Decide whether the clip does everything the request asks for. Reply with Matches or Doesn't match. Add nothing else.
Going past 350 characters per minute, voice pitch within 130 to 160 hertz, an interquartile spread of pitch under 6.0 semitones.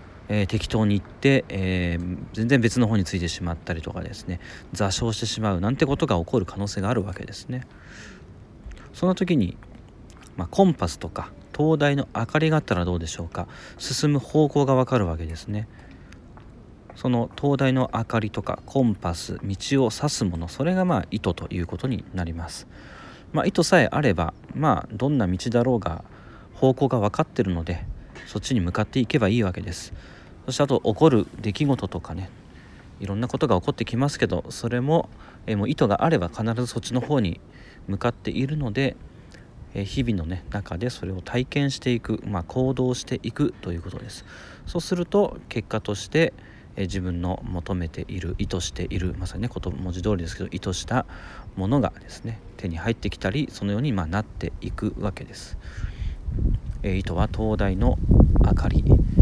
Doesn't match